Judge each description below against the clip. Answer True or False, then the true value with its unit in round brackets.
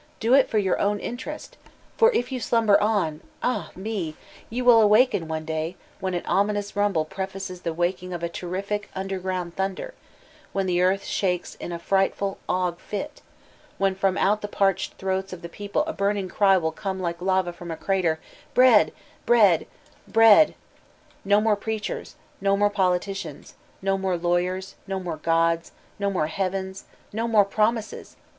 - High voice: True (195 Hz)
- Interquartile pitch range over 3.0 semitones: False (2.7 semitones)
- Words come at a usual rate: True (175 wpm)